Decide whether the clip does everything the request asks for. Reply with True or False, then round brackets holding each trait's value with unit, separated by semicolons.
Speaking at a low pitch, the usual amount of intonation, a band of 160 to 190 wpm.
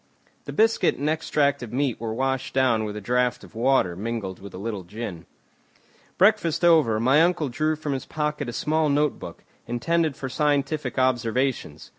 True (130 Hz; 4.7 semitones; 170 wpm)